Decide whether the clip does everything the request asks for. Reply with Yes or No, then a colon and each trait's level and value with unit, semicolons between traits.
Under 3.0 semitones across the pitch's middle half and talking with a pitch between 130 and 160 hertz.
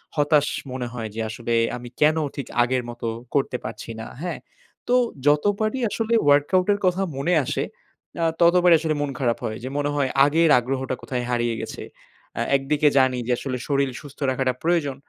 No: average, 4.3 semitones; medium, 140 Hz